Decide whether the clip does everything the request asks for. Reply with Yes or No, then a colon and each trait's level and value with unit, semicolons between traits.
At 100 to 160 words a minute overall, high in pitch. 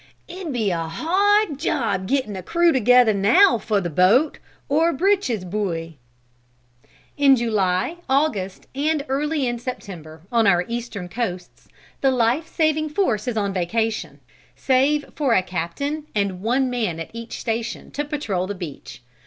Yes: average, 150 wpm; high, 235 Hz